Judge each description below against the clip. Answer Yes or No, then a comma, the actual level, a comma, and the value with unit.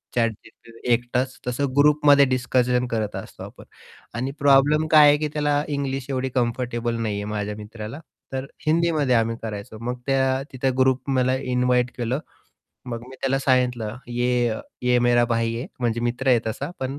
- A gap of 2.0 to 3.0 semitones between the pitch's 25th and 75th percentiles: Yes, narrow, 2.4 semitones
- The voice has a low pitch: Yes, low, 125 Hz